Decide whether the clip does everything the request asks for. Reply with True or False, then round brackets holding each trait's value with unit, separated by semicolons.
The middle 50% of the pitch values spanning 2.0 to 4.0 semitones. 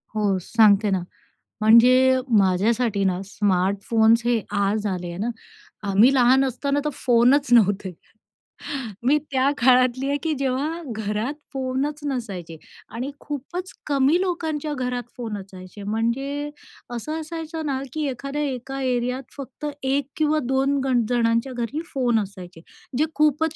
False (4.7 semitones)